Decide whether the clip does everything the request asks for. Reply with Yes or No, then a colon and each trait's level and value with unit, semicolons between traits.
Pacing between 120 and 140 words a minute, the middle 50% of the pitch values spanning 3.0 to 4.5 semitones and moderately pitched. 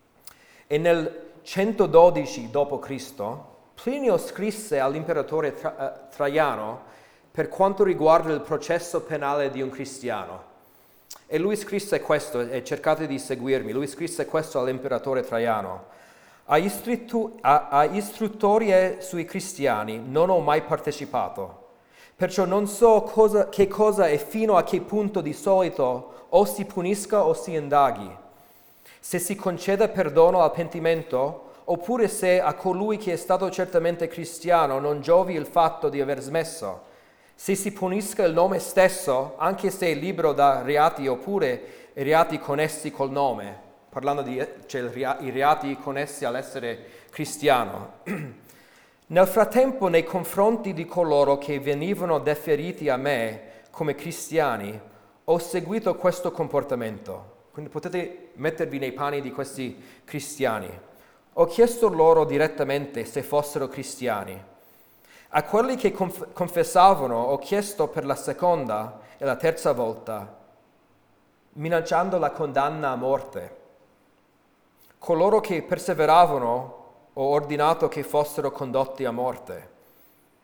No: average, 125 wpm; average, 5.1 semitones; medium, 160 Hz